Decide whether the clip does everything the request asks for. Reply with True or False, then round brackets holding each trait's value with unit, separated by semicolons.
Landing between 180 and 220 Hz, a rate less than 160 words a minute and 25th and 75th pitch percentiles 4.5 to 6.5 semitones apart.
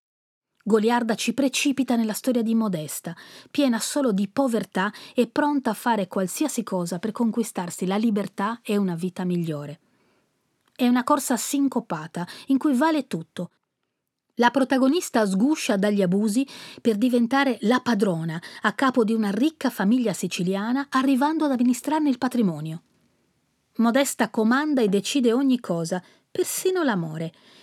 False (235 Hz; 135 wpm; 5.2 semitones)